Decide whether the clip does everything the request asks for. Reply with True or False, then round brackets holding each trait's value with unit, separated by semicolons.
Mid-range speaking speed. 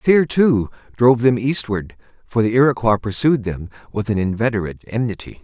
True (155 wpm)